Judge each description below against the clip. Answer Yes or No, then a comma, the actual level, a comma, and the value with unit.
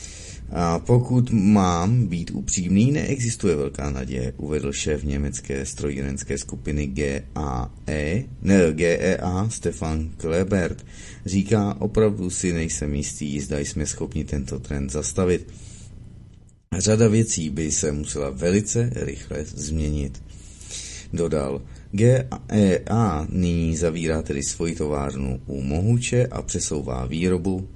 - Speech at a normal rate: No, slow, 105 wpm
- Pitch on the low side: Yes, very low, 85 Hz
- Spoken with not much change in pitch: No, wide, 5.7 semitones